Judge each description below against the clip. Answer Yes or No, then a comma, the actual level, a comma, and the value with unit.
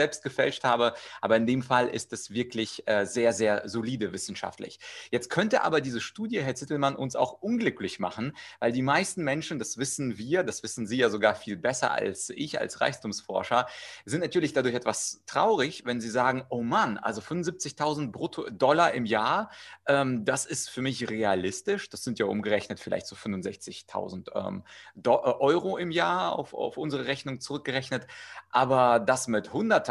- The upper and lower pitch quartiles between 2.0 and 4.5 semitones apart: Yes, average, 3.3 semitones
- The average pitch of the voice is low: Yes, low, 125 Hz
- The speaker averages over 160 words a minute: Yes, average, 175 wpm